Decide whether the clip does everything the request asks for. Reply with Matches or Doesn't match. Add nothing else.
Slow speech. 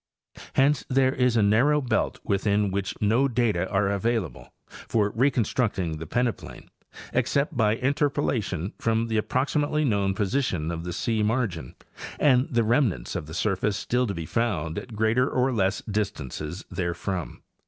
Doesn't match